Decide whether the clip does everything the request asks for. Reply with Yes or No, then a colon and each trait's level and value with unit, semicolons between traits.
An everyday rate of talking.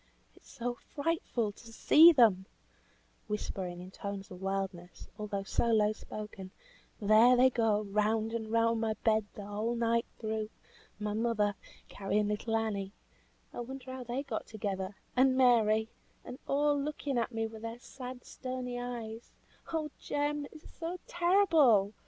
Yes: average, 155 wpm